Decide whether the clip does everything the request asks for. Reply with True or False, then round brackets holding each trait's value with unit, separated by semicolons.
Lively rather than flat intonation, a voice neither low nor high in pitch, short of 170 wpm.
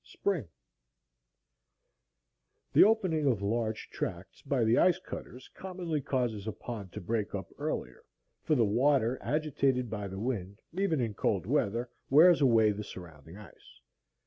False (6.1 semitones; 120 Hz; 145 wpm)